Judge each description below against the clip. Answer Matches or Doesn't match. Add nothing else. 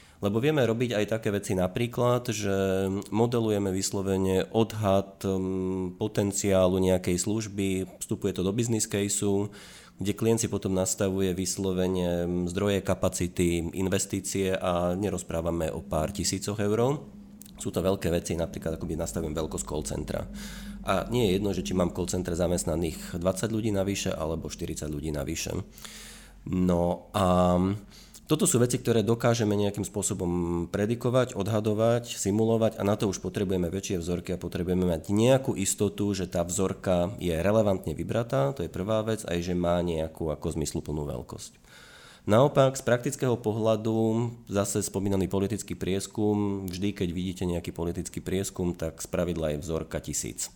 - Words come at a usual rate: Matches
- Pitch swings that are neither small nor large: Matches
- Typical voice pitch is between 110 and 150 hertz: Doesn't match